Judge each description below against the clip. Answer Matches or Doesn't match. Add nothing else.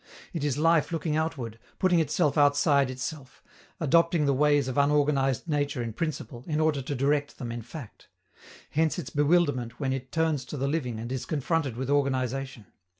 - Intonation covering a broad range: Doesn't match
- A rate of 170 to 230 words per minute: Matches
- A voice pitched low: Doesn't match